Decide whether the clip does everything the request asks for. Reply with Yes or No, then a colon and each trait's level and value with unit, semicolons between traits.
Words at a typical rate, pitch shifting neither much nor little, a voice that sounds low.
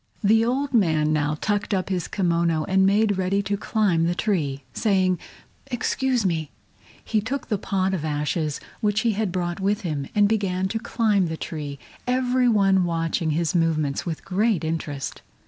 No: average, 170 wpm; average, 4.5 semitones; high, 190 Hz